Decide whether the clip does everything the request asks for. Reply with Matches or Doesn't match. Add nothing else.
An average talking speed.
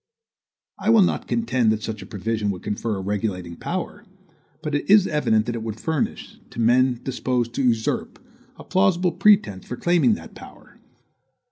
Matches